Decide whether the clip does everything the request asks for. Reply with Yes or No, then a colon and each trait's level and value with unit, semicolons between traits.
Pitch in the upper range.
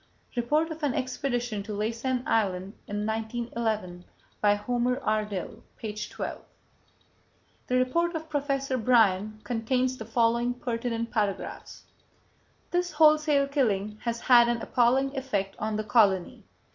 Yes: high, 235 Hz